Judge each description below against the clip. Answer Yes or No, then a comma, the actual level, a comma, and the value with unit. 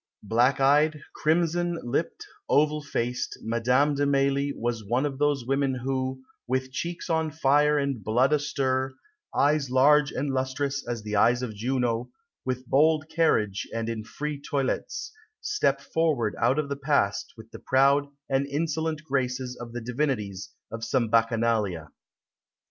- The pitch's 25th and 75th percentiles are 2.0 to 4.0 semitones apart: Yes, average, 3.4 semitones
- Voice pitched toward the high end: No, low, 135 Hz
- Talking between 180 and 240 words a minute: No, average, 150 wpm